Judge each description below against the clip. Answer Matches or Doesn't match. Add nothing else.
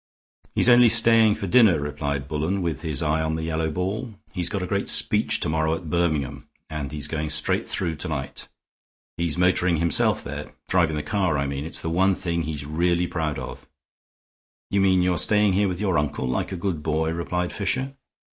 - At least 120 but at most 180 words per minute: Doesn't match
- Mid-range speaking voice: Doesn't match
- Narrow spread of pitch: Doesn't match